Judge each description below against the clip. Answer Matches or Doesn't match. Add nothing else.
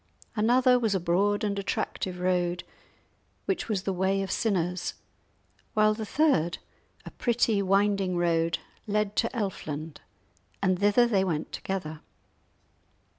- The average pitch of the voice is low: Doesn't match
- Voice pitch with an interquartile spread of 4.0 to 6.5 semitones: Doesn't match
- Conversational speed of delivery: Doesn't match